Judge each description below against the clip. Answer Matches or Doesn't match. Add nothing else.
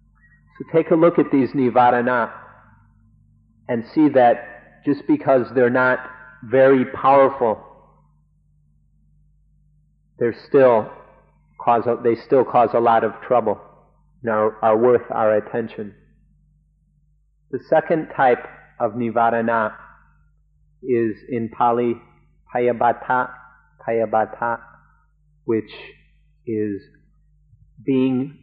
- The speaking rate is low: Matches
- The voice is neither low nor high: Doesn't match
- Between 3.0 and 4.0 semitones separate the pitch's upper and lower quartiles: Matches